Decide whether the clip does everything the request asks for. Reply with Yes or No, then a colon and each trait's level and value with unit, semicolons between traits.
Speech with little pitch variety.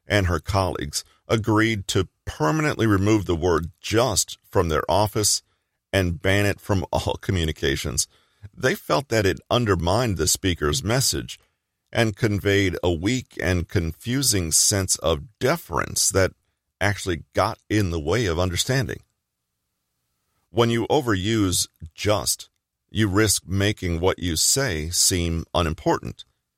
No: average, 4.0 semitones